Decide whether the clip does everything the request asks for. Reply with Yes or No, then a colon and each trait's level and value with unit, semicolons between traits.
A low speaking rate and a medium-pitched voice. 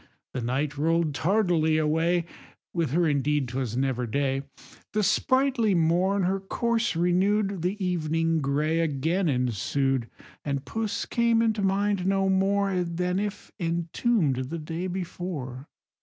Yes: slow, 130 wpm; medium, 170 Hz